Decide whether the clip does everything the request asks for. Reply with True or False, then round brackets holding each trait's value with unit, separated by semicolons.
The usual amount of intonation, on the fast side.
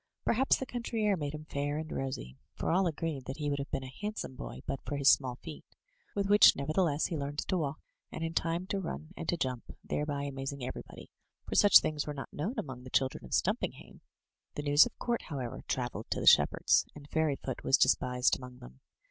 True (3.7 semitones; 220 wpm)